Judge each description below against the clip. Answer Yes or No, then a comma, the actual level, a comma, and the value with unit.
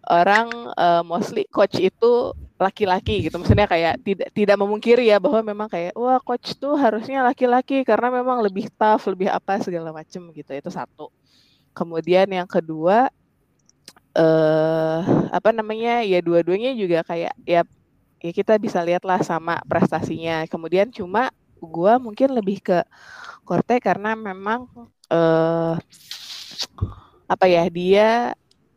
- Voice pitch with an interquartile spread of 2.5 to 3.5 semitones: No, average, 5.1 semitones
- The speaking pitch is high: Yes, high, 195 Hz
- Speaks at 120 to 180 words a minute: Yes, average, 135 wpm